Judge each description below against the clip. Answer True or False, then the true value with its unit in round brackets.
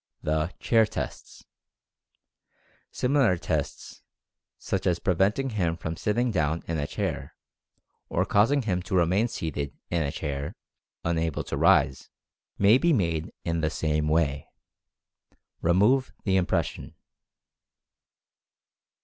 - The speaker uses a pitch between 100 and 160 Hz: False (85 Hz)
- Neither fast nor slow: False (115 wpm)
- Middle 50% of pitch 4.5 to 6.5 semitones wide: True (5.1 semitones)